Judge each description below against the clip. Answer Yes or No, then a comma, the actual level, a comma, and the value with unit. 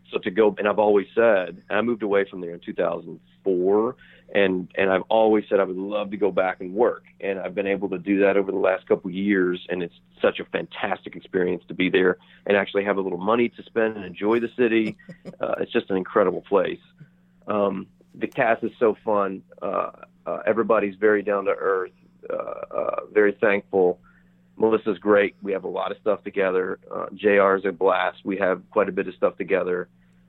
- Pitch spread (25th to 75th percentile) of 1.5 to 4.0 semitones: Yes, average, 2.9 semitones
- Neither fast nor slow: No, fast, 210 wpm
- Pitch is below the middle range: Yes, low, 100 Hz